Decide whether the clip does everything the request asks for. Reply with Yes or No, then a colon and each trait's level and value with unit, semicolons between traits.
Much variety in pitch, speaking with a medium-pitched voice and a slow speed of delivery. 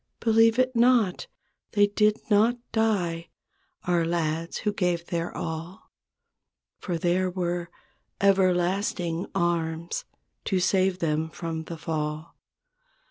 No: average, 3.4 semitones; medium, 175 Hz; slow, 110 wpm